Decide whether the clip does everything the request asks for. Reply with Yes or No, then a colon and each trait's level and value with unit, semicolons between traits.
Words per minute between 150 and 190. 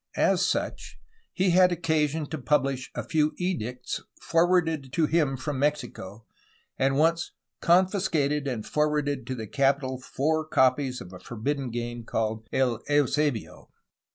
No: slow, 135 wpm